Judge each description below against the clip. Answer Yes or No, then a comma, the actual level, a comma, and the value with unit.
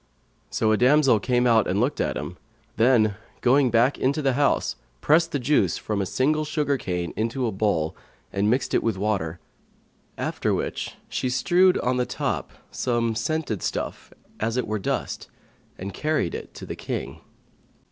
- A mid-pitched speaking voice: No, low, 120 Hz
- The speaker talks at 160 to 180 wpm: Yes, average, 170 wpm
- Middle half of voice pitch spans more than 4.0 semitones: Yes, average, 4.7 semitones